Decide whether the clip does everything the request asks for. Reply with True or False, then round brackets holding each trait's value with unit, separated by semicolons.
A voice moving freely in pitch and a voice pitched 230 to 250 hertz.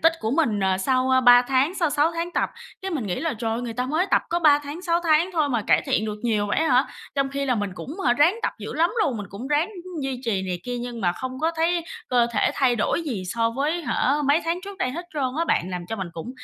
False (6.2 semitones; 265 Hz)